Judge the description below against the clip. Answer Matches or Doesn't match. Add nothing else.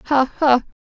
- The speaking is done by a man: Doesn't match